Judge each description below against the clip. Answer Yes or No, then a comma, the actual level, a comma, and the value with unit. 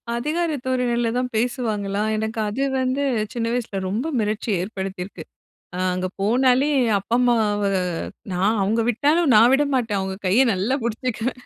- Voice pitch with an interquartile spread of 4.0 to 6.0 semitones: No, average, 3.6 semitones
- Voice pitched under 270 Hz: Yes, high, 230 Hz